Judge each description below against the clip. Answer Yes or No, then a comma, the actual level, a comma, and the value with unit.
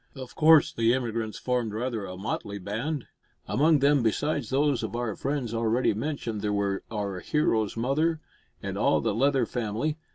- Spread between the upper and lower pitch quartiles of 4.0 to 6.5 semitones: Yes, average, 4.8 semitones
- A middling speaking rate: Yes, average, 165 wpm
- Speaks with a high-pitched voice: No, low, 120 Hz